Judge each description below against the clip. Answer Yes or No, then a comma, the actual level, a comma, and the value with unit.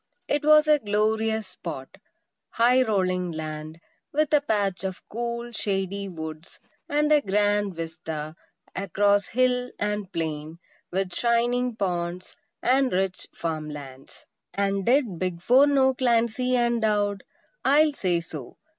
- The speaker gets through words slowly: Yes, slow, 130 wpm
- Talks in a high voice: Yes, high, 205 Hz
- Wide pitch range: Yes, wide, 5.7 semitones